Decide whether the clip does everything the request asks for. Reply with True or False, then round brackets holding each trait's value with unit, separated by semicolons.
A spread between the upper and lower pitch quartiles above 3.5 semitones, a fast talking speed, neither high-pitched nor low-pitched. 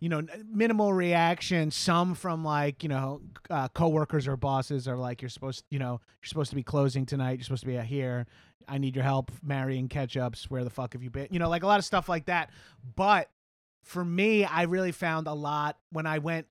True (4.5 semitones; 230 wpm; 145 Hz)